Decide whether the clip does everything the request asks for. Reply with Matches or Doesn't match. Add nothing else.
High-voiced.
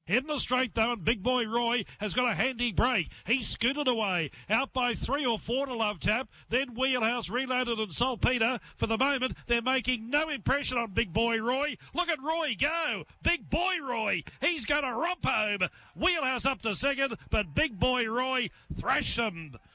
Matches